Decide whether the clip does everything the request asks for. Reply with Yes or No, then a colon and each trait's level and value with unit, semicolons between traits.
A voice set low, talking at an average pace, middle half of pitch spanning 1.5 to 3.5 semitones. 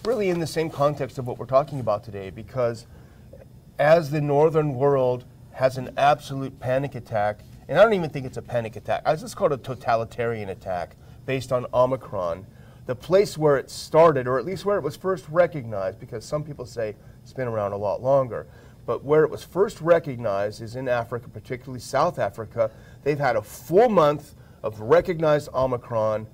No: low, 130 Hz; average, 190 wpm; average, 3.9 semitones